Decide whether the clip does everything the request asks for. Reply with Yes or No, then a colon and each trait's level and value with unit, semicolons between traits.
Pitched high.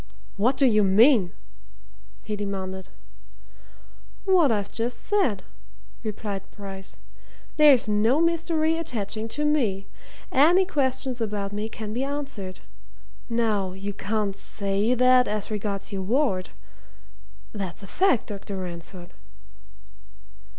Yes: high, 215 Hz